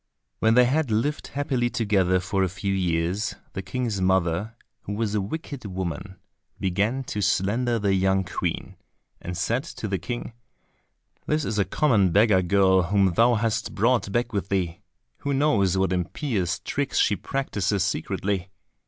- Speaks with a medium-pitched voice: No, low, 100 Hz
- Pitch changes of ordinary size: Yes, average, 4.0 semitones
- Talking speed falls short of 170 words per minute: Yes, average, 160 wpm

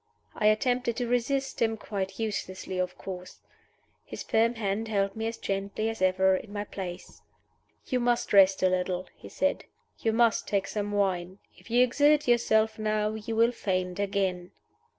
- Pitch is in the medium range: No, high, 210 Hz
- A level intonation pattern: No, average, 3.2 semitones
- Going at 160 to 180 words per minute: Yes, average, 170 wpm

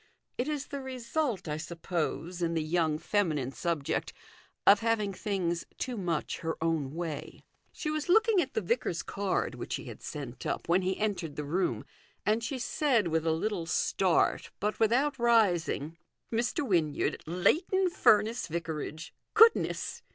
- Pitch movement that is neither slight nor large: No, wide, 6.3 semitones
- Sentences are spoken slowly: No, average, 160 wpm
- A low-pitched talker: No, high, 190 Hz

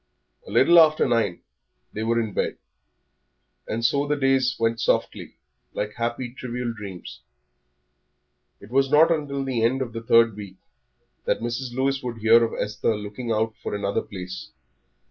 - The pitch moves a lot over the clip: No, average, 3.4 semitones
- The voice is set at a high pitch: No, low, 115 Hz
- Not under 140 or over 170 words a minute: Yes, average, 160 wpm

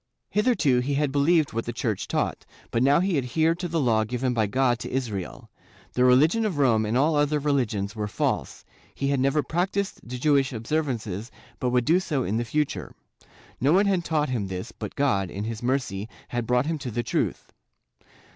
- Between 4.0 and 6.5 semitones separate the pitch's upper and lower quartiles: Yes, average, 4.7 semitones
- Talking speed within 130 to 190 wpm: No, average, 200 wpm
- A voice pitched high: No, low, 130 Hz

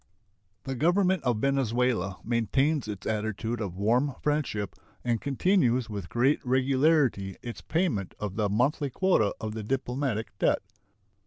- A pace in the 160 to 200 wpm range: No, slow, 135 wpm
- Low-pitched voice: Yes, low, 125 Hz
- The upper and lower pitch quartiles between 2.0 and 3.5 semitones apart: No, average, 4.6 semitones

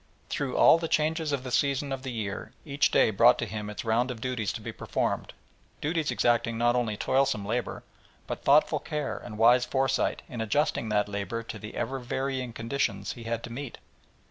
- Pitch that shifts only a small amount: No, average, 3.3 semitones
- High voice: No, low, 120 Hz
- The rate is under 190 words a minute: No, average, 195 wpm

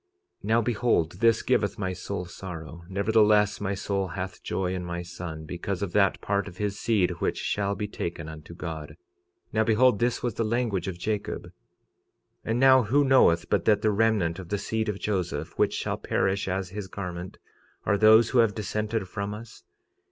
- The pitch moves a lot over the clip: No, average, 3.3 semitones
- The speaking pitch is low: Yes, low, 100 Hz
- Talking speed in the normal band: Yes, average, 195 wpm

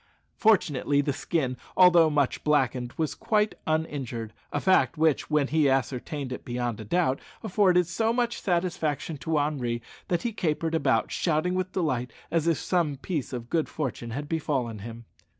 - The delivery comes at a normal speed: Yes, average, 165 wpm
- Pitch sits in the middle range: Yes, medium, 150 Hz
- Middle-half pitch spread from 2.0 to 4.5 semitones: No, average, 5.0 semitones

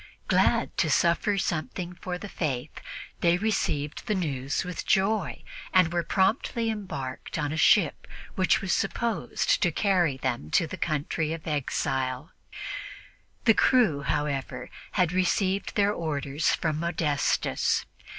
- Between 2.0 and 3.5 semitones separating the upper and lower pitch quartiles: No, average, 4.7 semitones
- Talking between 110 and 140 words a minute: Yes, slow, 135 wpm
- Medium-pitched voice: Yes, medium, 170 Hz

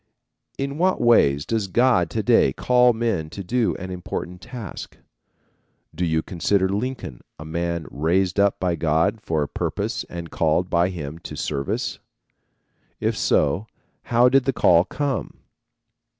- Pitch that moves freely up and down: Yes, wide, 6.3 semitones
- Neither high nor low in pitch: No, very low, 90 Hz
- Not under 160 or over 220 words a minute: No, average, 150 wpm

